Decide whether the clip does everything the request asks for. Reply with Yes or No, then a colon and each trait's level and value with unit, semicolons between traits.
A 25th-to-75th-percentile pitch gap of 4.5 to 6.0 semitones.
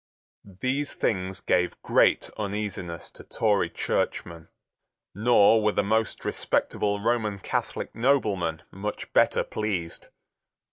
No: average, 3.0 semitones